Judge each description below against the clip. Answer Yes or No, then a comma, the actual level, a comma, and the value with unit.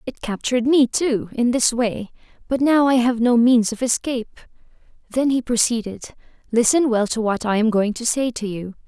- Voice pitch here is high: Yes, high, 235 Hz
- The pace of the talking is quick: No, average, 195 wpm